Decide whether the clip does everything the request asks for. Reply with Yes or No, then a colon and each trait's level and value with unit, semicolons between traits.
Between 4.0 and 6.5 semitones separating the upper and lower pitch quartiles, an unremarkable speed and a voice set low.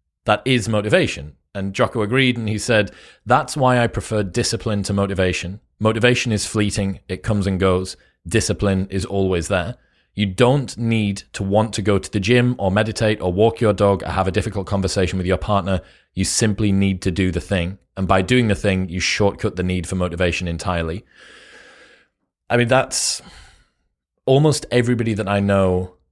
No: average, 3.0 semitones; average, 180 wpm; low, 100 Hz